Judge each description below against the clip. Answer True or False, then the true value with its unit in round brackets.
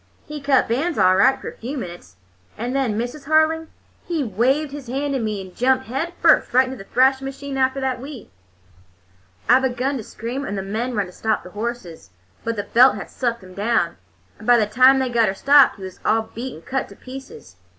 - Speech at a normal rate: False (225 wpm)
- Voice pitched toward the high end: True (250 Hz)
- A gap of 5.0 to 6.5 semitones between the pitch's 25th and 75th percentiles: False (3.9 semitones)